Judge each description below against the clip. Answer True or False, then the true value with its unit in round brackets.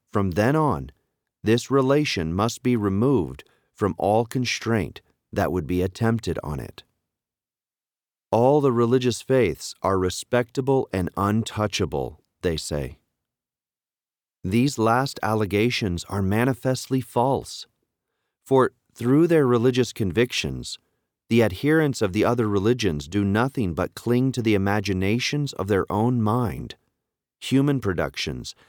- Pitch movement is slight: False (4.6 semitones)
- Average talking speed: False (120 wpm)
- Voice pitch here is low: True (115 Hz)